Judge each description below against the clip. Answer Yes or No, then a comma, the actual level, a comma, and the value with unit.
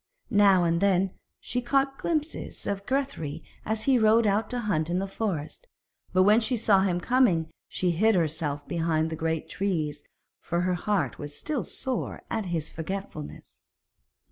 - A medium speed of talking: Yes, average, 165 wpm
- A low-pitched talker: No, high, 190 Hz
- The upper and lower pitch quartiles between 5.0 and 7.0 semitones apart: Yes, wide, 5.5 semitones